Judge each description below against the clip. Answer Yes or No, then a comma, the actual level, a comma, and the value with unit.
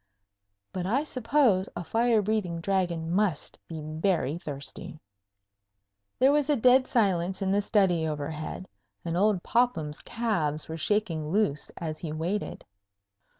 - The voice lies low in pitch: No, medium, 185 Hz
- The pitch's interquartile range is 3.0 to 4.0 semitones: No, average, 5.2 semitones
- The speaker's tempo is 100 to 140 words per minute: Yes, slow, 135 wpm